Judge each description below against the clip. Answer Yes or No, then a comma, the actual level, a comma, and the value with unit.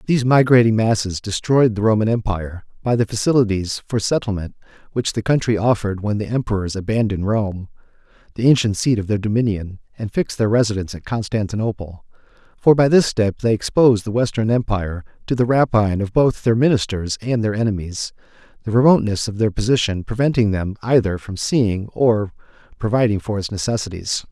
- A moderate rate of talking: Yes, average, 165 wpm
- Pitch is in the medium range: No, low, 110 Hz